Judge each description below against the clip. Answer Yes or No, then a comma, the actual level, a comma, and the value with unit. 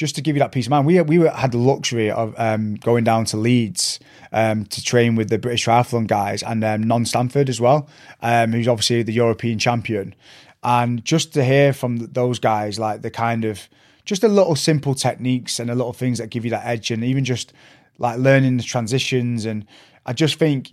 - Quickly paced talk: Yes, fast, 220 wpm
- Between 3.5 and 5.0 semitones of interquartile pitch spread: No, average, 2.9 semitones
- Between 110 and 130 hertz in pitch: Yes, low, 120 Hz